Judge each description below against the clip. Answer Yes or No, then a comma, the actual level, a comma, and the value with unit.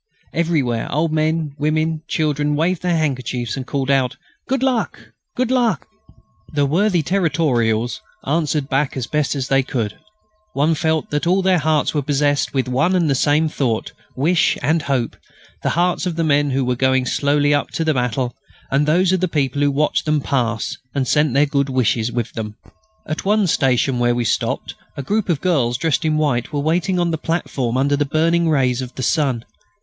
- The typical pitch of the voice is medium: Yes, medium, 145 Hz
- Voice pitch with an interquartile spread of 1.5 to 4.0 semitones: Yes, average, 3.7 semitones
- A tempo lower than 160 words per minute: No, average, 190 wpm